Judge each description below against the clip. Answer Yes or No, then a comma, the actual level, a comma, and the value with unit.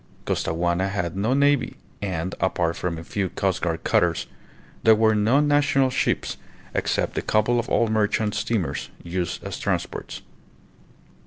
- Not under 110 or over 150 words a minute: Yes, average, 140 wpm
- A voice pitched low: Yes, low, 105 Hz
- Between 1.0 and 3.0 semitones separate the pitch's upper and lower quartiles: No, average, 4.8 semitones